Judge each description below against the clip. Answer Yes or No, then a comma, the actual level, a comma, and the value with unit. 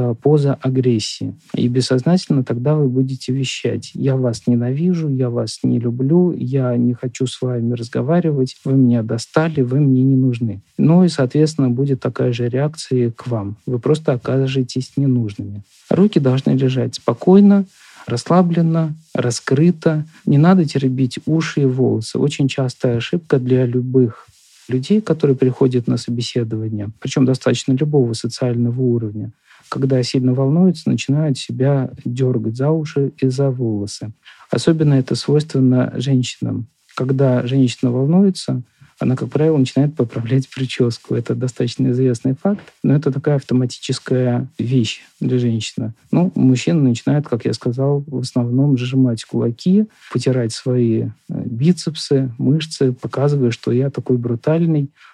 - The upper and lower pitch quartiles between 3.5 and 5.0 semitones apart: No, average, 2.8 semitones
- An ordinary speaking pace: Yes, average, 135 wpm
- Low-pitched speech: Yes, low, 130 Hz